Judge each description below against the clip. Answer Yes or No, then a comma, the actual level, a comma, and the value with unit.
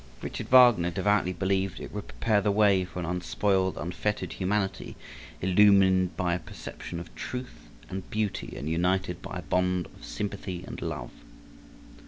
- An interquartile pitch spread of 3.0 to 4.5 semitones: No, narrow, 2.4 semitones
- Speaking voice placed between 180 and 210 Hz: No, very low, 95 Hz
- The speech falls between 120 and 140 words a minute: No, average, 155 wpm